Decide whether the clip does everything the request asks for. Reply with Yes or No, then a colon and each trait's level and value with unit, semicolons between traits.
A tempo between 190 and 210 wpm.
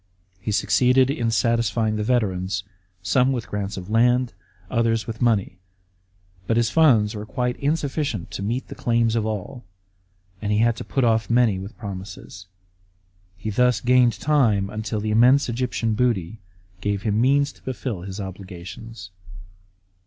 No: average, 155 wpm